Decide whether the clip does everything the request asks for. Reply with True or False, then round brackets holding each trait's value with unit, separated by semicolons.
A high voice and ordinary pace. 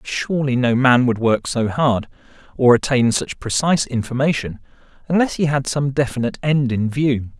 False (130 Hz; 160 wpm)